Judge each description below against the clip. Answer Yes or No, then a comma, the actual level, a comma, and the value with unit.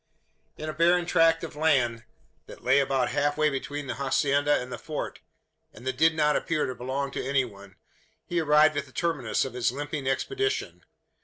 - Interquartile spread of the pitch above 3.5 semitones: No, average, 3.1 semitones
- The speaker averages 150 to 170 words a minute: No, average, 190 wpm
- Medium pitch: Yes, medium, 145 Hz